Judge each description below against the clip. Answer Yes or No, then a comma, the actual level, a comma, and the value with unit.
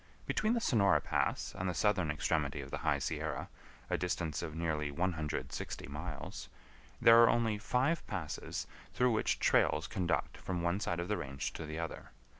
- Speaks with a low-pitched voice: Yes, very low, 85 Hz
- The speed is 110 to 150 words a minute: No, average, 175 wpm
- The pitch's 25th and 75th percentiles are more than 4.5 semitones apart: Yes, average, 5.2 semitones